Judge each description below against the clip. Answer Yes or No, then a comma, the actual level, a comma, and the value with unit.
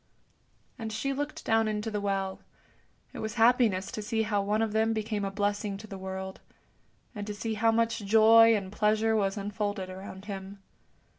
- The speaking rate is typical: Yes, average, 180 wpm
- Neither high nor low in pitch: No, high, 210 Hz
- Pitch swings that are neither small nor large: No, narrow, 2.0 semitones